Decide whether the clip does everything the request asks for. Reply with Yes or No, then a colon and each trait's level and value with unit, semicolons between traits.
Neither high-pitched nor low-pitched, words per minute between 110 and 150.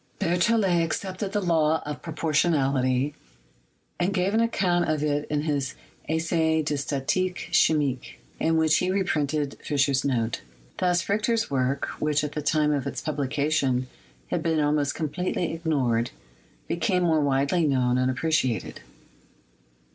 Yes: medium, 155 Hz; average, 140 wpm